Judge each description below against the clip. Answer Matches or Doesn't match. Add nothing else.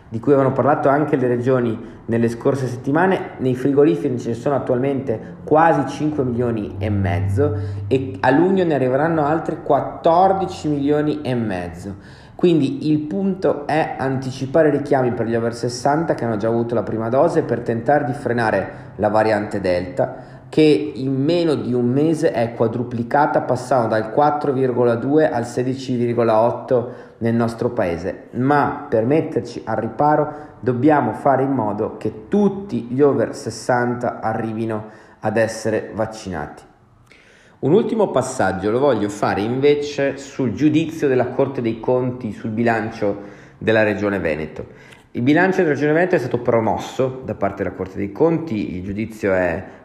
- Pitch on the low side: Matches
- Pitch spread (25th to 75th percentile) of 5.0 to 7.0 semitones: Doesn't match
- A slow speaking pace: Doesn't match